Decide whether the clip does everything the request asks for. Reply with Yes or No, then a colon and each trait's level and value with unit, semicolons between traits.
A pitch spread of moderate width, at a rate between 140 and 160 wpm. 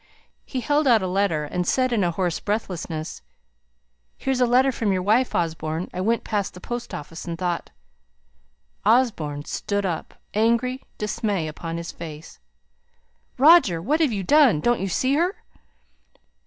No: wide, 6.7 semitones; average, 155 wpm